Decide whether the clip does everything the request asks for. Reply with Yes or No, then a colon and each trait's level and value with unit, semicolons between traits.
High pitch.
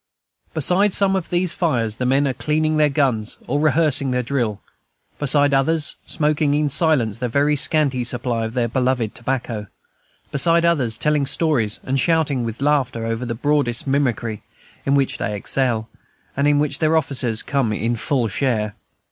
No: low, 135 Hz